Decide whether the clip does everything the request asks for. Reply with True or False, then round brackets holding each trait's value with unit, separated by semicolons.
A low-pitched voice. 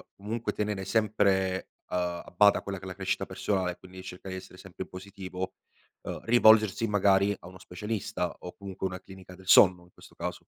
True (95 Hz)